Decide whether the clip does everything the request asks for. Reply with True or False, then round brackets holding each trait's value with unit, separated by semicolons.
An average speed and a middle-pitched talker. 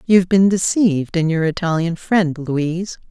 True (155 wpm; 175 Hz)